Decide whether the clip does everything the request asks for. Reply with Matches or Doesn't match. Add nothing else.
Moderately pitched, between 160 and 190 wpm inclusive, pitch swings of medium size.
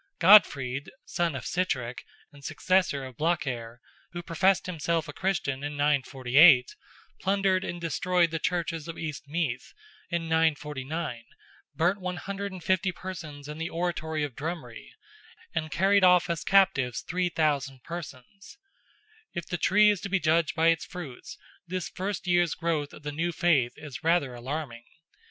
Doesn't match